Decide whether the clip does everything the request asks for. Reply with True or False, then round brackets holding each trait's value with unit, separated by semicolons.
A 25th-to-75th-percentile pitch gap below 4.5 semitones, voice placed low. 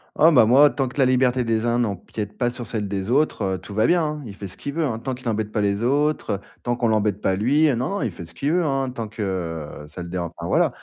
False (5.0 semitones; 115 Hz)